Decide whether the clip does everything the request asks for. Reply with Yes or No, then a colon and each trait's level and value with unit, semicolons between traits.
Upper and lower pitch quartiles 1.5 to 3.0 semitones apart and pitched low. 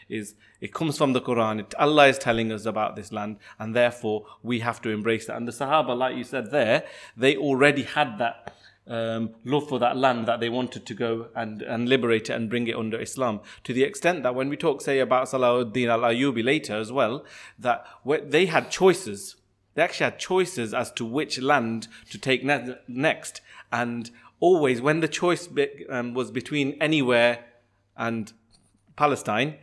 No: average, 3.5 semitones; low, 120 Hz